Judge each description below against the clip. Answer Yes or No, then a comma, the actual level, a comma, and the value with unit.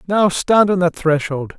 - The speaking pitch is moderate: Yes, medium, 175 Hz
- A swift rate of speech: No, average, 190 wpm